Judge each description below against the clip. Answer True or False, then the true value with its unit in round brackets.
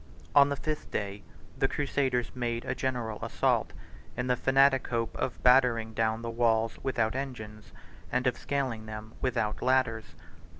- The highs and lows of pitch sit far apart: False (2.9 semitones)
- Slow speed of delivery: False (155 wpm)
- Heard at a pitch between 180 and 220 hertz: False (120 Hz)